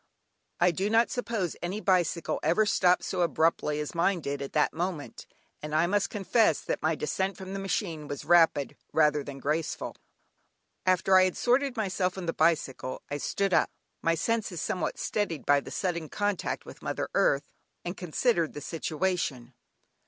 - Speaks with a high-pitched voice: No, medium, 175 Hz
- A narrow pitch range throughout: No, average, 4.0 semitones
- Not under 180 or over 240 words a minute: No, average, 170 wpm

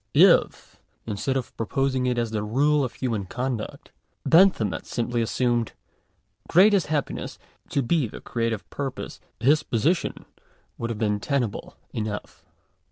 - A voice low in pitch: Yes, low, 120 Hz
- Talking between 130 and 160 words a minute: Yes, average, 150 wpm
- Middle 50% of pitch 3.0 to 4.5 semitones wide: Yes, average, 3.9 semitones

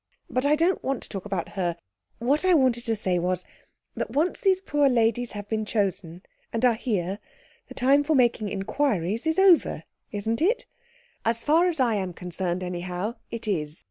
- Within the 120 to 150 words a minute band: No, average, 185 wpm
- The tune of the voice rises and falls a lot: Yes, wide, 7.0 semitones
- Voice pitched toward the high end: Yes, high, 225 Hz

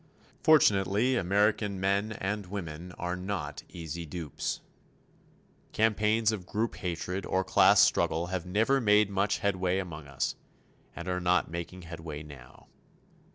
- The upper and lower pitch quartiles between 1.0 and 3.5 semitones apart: Yes, average, 3.2 semitones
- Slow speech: Yes, slow, 130 wpm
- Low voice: Yes, very low, 95 Hz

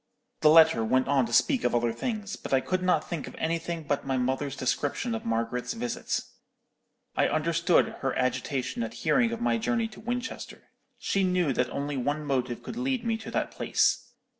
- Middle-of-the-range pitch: Yes, medium, 155 Hz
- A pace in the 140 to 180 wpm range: No, average, 195 wpm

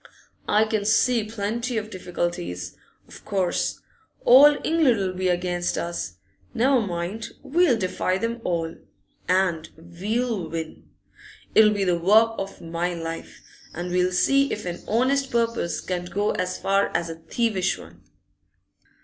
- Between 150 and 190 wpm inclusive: No, average, 140 wpm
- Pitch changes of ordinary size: Yes, average, 4.6 semitones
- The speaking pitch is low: No, high, 190 Hz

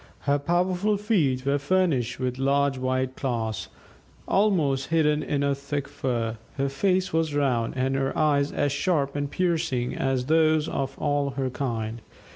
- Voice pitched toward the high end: No, medium, 140 Hz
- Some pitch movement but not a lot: Yes, average, 3.2 semitones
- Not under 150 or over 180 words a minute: Yes, average, 155 wpm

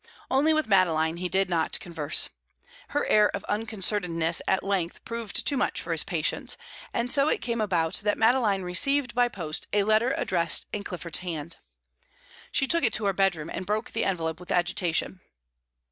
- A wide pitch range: No, average, 4.8 semitones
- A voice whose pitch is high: Yes, high, 195 Hz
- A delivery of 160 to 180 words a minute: Yes, average, 175 wpm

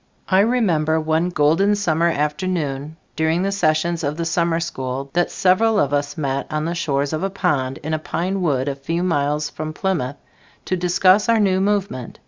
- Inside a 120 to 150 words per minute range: No, average, 185 wpm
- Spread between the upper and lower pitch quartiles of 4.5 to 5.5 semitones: No, average, 4.0 semitones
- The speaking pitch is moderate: Yes, medium, 165 Hz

